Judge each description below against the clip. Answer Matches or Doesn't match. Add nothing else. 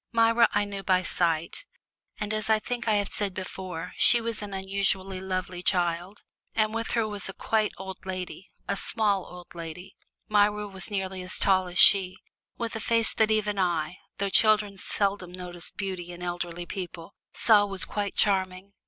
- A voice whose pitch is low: Doesn't match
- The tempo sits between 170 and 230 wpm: Matches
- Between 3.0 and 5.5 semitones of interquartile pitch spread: Doesn't match